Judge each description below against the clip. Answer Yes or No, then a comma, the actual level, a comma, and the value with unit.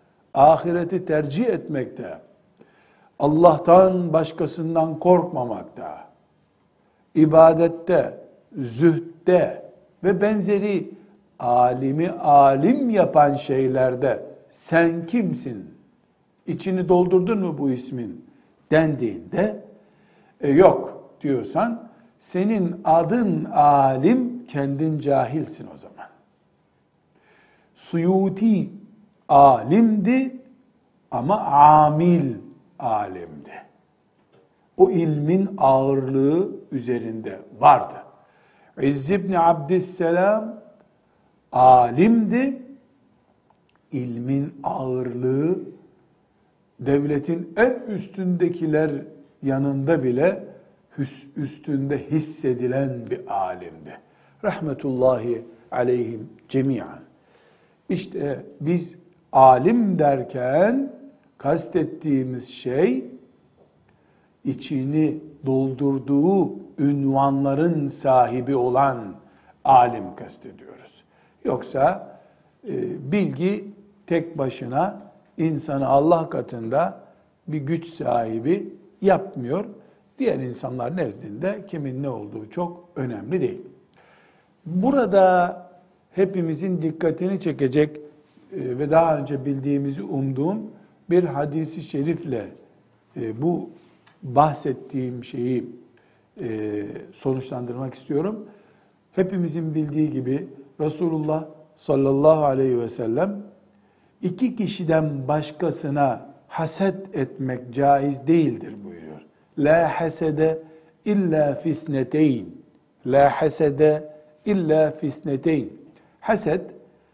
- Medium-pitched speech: Yes, medium, 155 Hz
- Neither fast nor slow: No, slow, 70 wpm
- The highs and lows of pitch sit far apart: No, average, 5.0 semitones